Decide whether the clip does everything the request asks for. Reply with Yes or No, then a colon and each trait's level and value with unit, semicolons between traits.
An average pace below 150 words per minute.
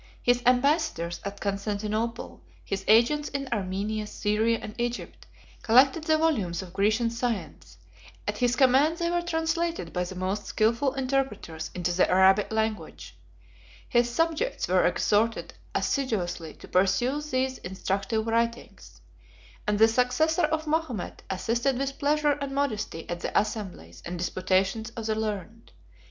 Yes: average, 140 wpm